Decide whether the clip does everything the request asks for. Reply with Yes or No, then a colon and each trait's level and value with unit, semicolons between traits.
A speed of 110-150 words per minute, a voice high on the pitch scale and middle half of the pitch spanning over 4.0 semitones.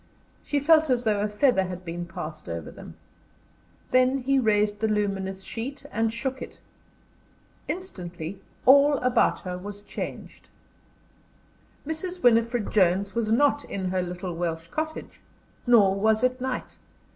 Yes: average, 140 wpm; high, 215 Hz; wide, 5.4 semitones